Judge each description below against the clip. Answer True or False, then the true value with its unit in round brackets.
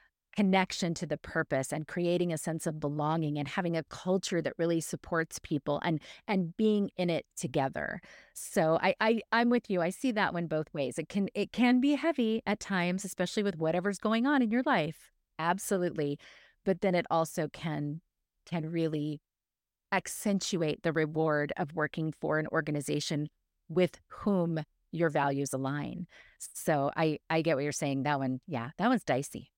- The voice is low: False (165 Hz)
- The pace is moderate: True (175 wpm)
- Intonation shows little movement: False (4.0 semitones)